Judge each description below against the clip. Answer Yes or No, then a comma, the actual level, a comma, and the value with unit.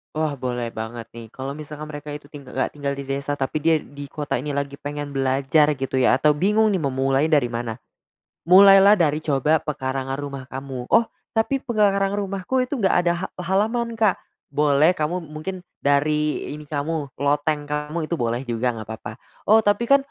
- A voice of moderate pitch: Yes, medium, 145 Hz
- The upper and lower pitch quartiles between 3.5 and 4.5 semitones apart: Yes, average, 4.2 semitones